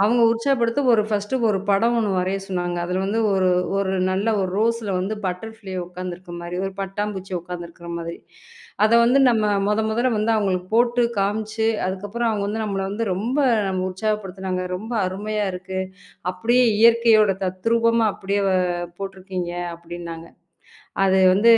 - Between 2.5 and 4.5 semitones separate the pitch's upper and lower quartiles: Yes, average, 3.2 semitones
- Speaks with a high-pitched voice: Yes, high, 200 Hz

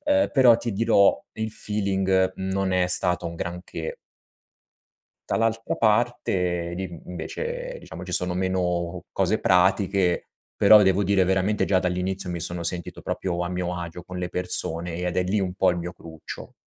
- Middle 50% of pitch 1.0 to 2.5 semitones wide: Yes, narrow, 2.1 semitones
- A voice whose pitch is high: No, very low, 90 Hz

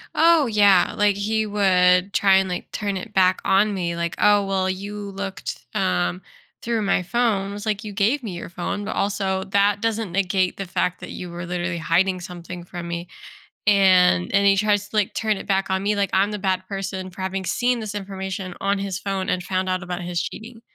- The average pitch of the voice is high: Yes, high, 195 Hz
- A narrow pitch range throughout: Yes, narrow, 2.1 semitones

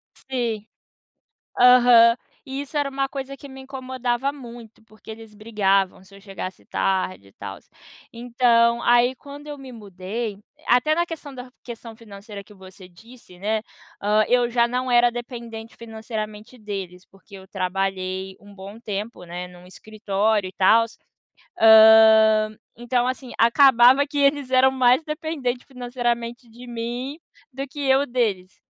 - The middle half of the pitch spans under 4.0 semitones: Yes, average, 3.6 semitones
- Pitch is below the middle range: No, high, 235 Hz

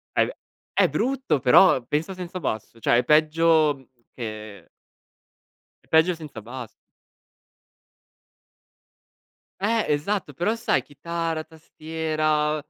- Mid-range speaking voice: Yes, medium, 155 Hz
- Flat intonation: No, average, 4.0 semitones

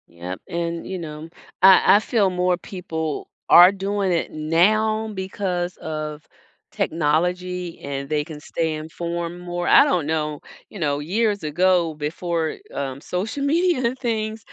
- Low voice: No, medium, 175 Hz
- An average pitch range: Yes, average, 3.8 semitones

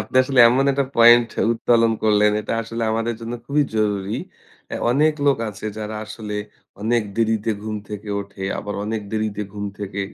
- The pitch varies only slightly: Yes, narrow, 2.0 semitones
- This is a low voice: Yes, low, 110 Hz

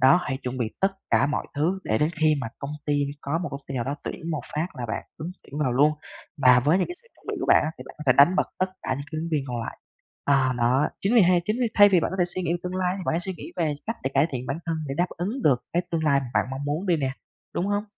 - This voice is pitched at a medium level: Yes, medium, 155 Hz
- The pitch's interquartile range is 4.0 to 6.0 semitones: Yes, average, 5.1 semitones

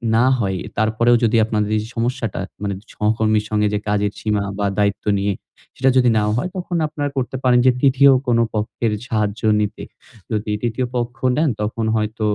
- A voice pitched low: Yes, low, 110 Hz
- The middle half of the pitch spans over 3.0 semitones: No, narrow, 2.6 semitones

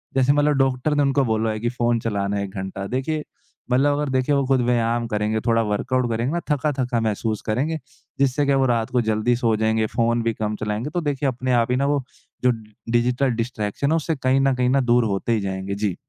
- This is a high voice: No, low, 120 Hz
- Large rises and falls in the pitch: No, average, 3.5 semitones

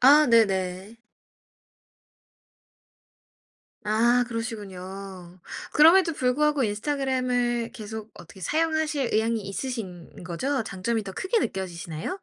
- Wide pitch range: Yes, wide, 5.8 semitones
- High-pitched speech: Yes, high, 230 Hz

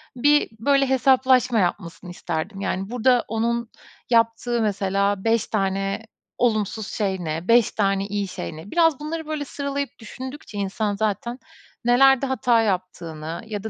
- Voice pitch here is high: Yes, high, 220 Hz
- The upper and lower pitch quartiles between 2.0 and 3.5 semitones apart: No, average, 4.5 semitones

